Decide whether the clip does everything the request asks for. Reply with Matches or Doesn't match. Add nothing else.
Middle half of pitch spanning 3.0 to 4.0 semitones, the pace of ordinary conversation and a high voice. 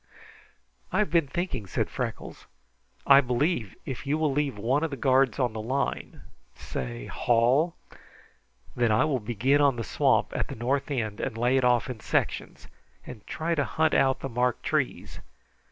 Doesn't match